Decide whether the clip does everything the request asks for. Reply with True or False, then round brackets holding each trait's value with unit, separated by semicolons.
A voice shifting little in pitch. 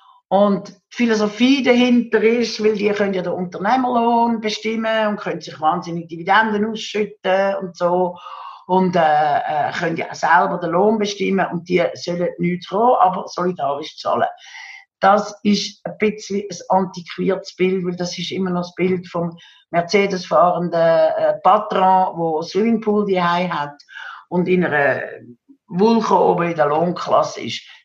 False (3.6 semitones)